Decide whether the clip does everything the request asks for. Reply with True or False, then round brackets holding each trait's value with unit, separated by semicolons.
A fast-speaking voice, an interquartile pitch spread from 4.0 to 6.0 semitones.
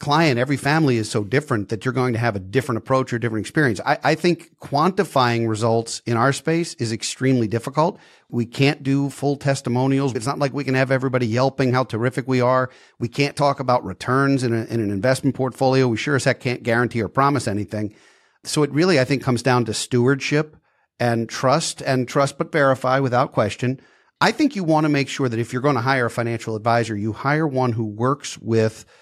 False (215 wpm; 3.0 semitones)